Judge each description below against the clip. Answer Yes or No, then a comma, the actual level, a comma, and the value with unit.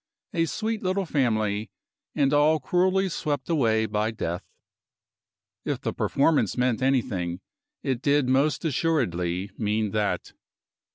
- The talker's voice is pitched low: Yes, low, 130 Hz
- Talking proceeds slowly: Yes, slow, 120 wpm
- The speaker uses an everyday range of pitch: No, wide, 6.5 semitones